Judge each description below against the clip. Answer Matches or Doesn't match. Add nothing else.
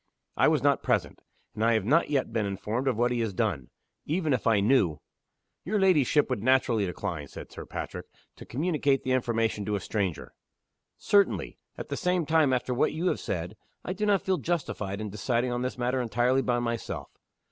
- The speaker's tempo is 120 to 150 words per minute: Doesn't match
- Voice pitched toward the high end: Doesn't match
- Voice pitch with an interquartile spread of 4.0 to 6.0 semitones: Matches